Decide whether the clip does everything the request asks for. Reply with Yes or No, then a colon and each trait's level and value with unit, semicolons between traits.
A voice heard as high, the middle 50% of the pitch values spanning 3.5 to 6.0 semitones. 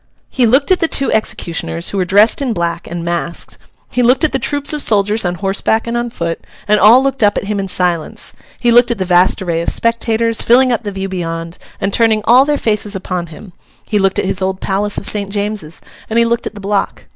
Yes: high, 205 Hz; average, 4.3 semitones